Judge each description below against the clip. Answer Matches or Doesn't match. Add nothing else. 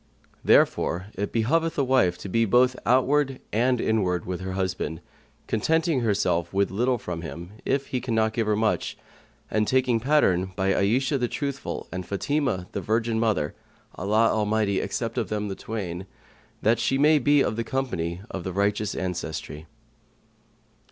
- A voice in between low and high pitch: Doesn't match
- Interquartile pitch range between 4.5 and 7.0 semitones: Matches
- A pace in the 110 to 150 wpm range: Doesn't match